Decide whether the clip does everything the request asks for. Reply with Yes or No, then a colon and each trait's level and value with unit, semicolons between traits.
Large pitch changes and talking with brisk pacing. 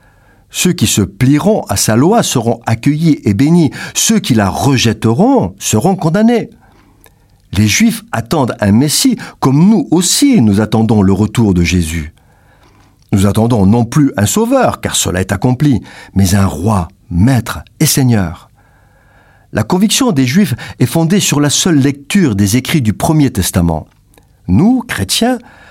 No: wide, 8.1 semitones; average, 150 wpm